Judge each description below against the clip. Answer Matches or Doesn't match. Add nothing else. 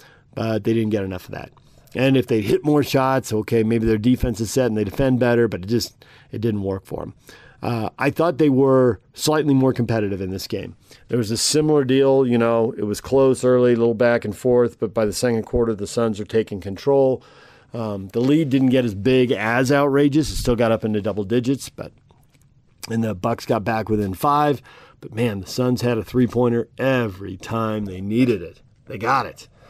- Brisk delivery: Matches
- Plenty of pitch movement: Doesn't match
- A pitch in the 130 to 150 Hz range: Doesn't match